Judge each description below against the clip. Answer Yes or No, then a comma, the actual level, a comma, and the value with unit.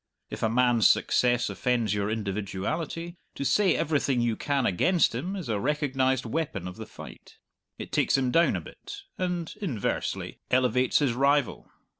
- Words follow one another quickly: No, average, 160 wpm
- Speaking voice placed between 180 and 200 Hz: No, low, 130 Hz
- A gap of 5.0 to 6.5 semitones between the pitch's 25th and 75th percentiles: Yes, wide, 5.5 semitones